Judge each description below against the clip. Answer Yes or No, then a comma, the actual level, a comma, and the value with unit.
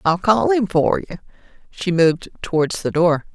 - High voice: No, medium, 180 Hz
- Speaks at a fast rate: No, average, 180 wpm